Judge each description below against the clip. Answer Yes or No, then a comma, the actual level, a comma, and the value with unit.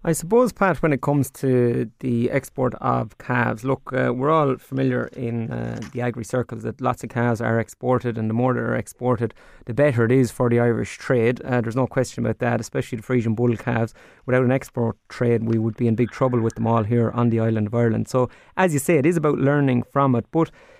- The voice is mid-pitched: No, low, 120 Hz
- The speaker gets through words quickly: Yes, fast, 235 wpm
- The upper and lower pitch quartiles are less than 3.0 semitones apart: Yes, narrow, 2.4 semitones